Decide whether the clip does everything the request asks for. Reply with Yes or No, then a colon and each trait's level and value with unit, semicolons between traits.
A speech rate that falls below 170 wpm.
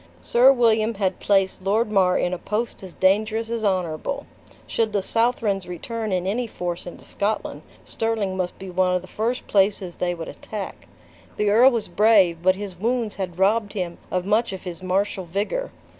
No: average, 185 wpm